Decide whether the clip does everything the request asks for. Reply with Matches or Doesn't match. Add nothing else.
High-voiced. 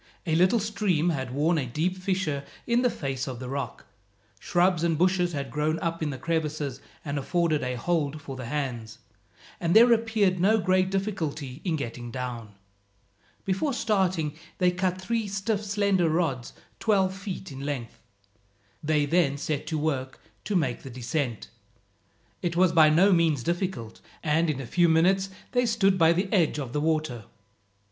Doesn't match